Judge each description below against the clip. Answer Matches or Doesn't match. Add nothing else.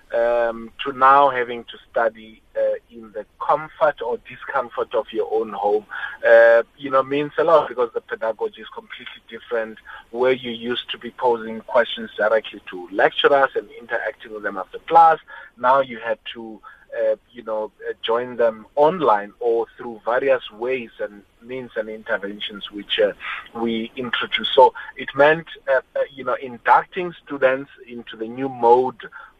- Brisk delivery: Doesn't match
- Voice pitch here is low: Matches